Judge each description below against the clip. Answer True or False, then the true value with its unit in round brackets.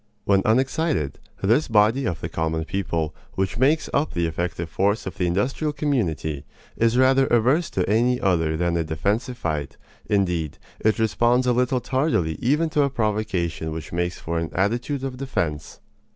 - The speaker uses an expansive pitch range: True (7.3 semitones)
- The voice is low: True (105 Hz)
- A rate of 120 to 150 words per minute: False (165 wpm)